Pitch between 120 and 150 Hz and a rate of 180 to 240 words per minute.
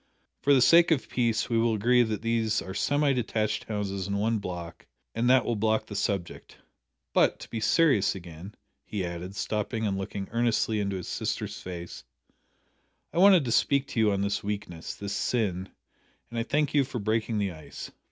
No: low, 110 Hz; average, 190 wpm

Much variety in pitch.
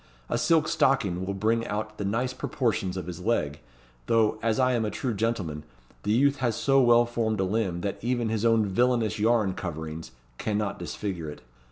No: average, 3.9 semitones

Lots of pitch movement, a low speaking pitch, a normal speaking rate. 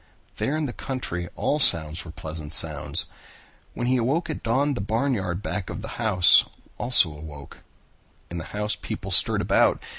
Yes: wide, 7.6 semitones; low, 105 Hz; average, 170 wpm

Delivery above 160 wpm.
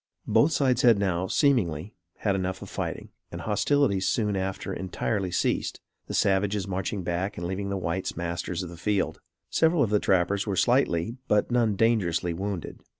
Yes: average, 170 wpm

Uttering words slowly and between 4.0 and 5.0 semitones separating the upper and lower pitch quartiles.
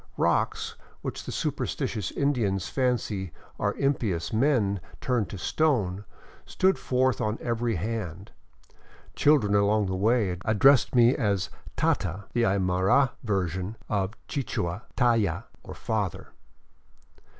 Yes: slow, 125 wpm; average, 4.4 semitones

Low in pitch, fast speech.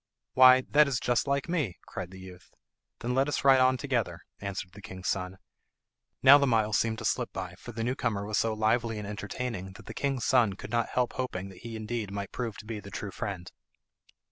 Yes: low, 110 Hz; fast, 220 wpm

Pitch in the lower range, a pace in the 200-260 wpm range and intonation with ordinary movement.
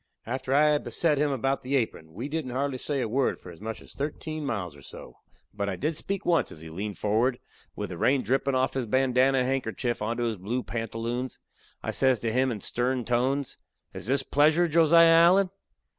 Yes: low, 130 Hz; fast, 205 wpm; average, 3.9 semitones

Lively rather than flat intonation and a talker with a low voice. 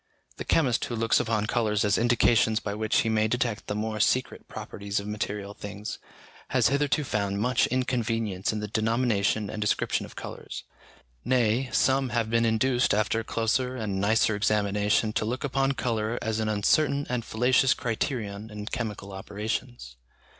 No: narrow, 2.6 semitones; low, 110 Hz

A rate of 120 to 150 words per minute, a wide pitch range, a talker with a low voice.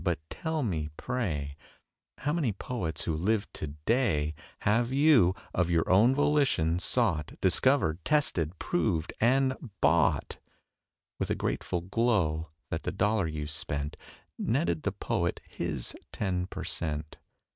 Yes: slow, 135 wpm; wide, 7.5 semitones; very low, 90 Hz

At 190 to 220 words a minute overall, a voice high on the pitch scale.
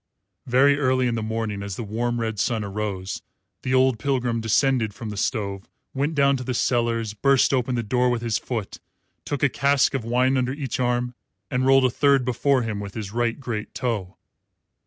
No: average, 200 wpm; low, 120 Hz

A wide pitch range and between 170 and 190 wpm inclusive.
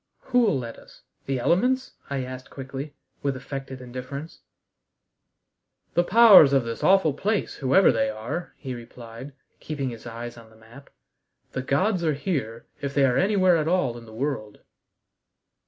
No: wide, 6.0 semitones; average, 155 wpm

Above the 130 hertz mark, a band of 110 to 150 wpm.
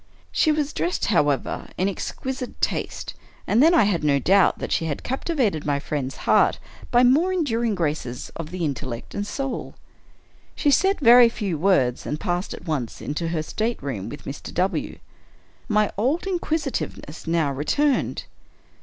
No: high, 190 Hz; average, 165 wpm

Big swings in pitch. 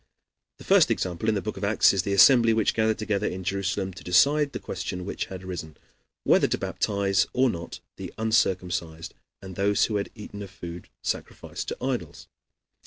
No: average, 3.0 semitones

